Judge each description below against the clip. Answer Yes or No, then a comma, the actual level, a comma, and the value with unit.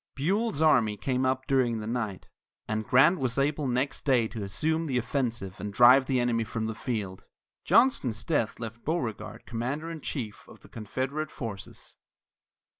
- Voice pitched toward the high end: No, low, 125 Hz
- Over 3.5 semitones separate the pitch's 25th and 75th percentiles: Yes, average, 4.0 semitones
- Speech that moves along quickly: No, average, 165 wpm